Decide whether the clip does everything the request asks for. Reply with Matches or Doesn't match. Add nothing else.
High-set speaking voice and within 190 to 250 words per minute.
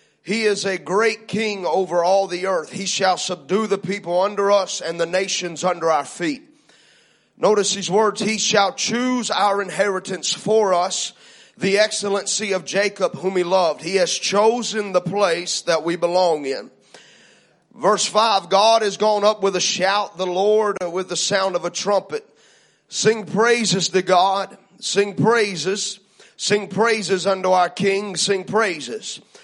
Doesn't match